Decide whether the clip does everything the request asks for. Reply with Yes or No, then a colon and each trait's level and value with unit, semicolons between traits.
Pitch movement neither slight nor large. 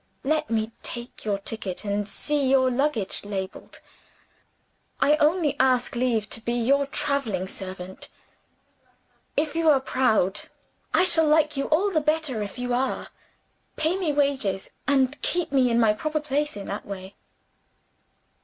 No: wide, 5.9 semitones